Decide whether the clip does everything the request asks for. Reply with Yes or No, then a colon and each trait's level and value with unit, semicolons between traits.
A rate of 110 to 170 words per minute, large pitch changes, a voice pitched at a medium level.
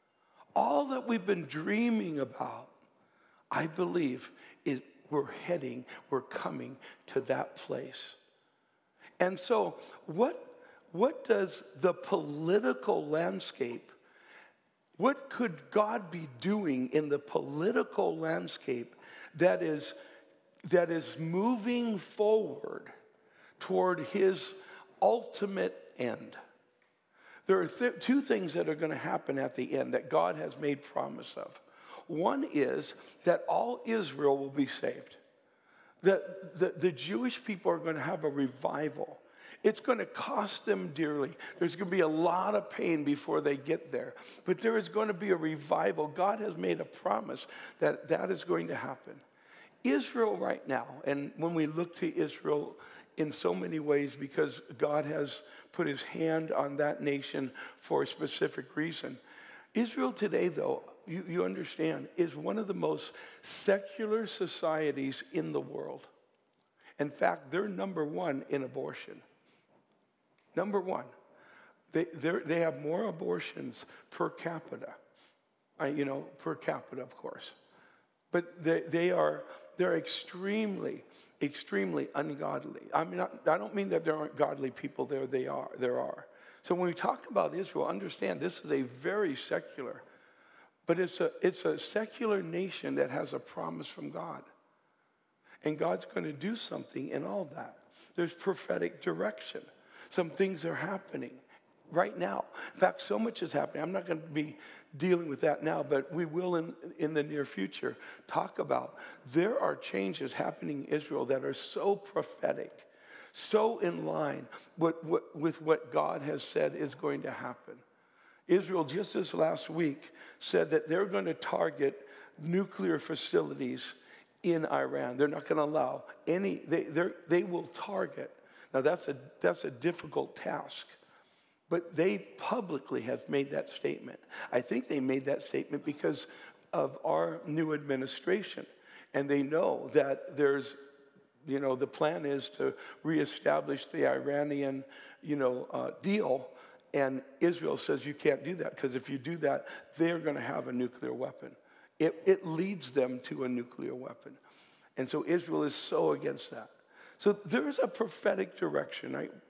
Yes: average, 155 wpm; wide, 5.9 semitones; medium, 170 Hz